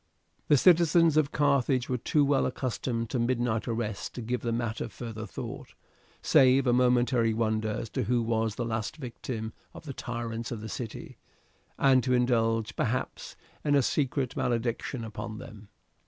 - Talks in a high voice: No, low, 120 Hz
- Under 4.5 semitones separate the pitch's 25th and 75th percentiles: Yes, narrow, 2.4 semitones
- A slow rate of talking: No, average, 165 wpm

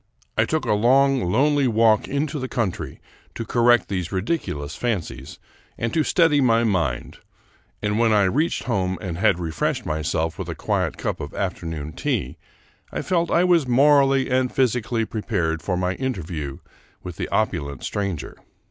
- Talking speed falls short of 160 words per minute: No, average, 165 wpm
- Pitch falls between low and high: No, low, 110 Hz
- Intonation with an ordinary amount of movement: No, wide, 7.4 semitones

